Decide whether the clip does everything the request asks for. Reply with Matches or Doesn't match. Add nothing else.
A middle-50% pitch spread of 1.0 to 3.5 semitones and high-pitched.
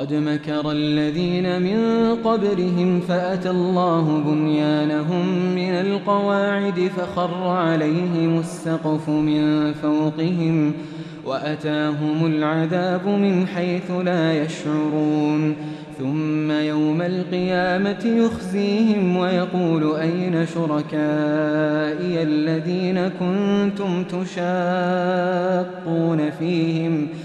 Doesn't match